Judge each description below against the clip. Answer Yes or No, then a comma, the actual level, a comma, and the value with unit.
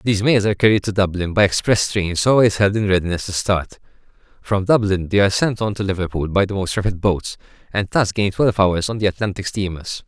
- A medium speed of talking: No, fast, 220 wpm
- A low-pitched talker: Yes, low, 100 Hz